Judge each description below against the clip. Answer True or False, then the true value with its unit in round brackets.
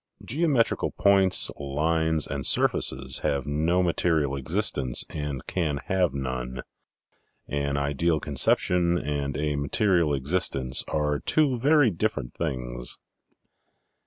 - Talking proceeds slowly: True (105 wpm)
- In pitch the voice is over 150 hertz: False (75 Hz)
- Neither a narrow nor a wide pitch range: True (4.5 semitones)